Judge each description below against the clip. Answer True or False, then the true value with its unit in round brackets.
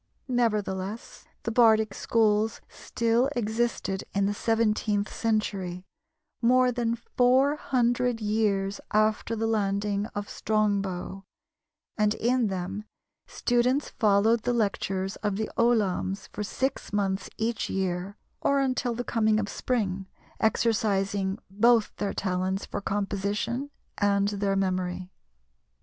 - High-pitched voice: True (210 Hz)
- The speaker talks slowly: True (115 wpm)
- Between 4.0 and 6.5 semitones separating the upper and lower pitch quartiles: False (3.0 semitones)